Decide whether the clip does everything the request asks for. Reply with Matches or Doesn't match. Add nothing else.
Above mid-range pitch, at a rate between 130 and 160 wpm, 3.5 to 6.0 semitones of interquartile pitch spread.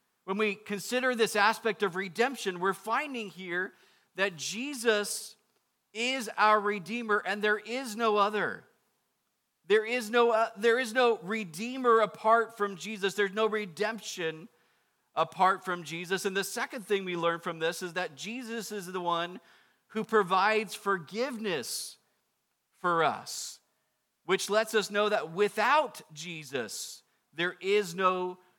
Doesn't match